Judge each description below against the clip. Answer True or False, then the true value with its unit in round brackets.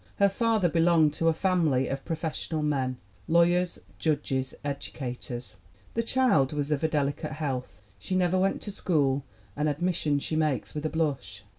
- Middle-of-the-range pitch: True (155 Hz)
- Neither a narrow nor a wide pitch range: True (4.0 semitones)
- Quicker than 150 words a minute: True (160 wpm)